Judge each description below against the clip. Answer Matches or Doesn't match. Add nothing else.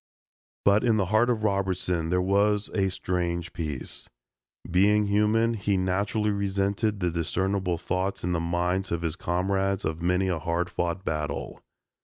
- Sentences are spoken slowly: Doesn't match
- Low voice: Matches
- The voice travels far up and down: Doesn't match